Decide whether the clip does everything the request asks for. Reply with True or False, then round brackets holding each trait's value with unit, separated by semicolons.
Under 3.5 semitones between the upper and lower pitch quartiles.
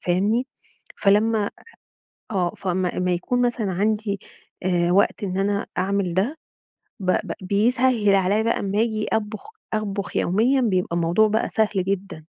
True (2.9 semitones)